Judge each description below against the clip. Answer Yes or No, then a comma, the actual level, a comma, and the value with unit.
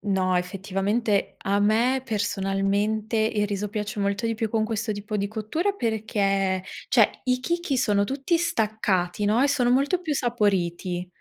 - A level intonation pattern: No, average, 3.3 semitones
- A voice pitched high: Yes, high, 210 Hz